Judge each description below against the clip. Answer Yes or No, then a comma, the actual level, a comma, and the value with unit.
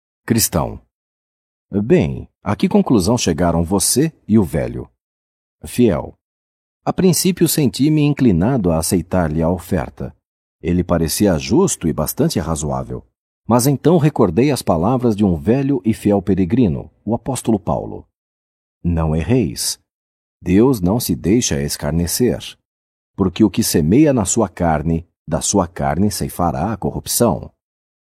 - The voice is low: Yes, very low, 95 Hz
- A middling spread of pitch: No, wide, 7.1 semitones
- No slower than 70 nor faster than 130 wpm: Yes, average, 125 wpm